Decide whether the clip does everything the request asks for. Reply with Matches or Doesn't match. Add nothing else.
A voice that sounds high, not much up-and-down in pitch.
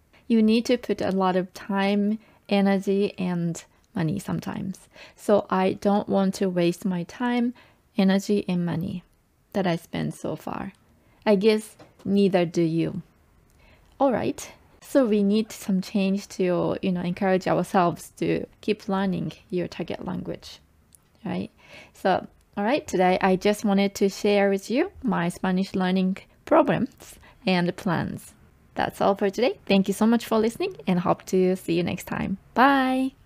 Matches